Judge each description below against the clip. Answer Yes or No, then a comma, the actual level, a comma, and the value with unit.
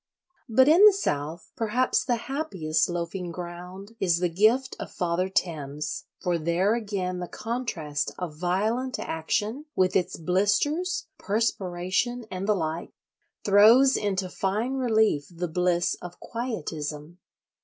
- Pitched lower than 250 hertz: Yes, medium, 185 Hz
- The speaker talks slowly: Yes, slow, 130 wpm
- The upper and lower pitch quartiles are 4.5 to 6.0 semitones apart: Yes, average, 5.0 semitones